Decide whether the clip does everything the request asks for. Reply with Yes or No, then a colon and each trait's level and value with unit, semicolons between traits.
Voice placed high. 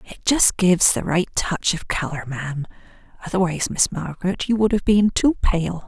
No: medium, 180 Hz